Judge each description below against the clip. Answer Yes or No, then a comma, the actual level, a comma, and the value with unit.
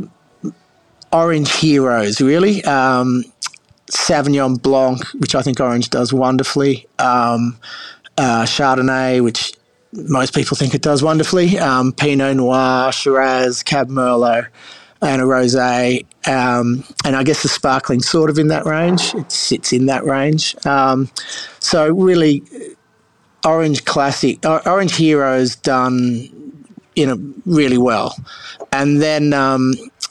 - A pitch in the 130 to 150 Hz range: Yes, low, 135 Hz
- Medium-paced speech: No, slow, 120 wpm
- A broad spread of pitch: No, narrow, 2.6 semitones